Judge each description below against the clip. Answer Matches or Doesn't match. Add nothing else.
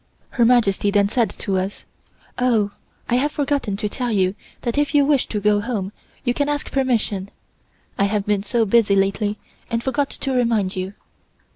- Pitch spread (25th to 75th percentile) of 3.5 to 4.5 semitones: Matches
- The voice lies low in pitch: Doesn't match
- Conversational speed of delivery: Matches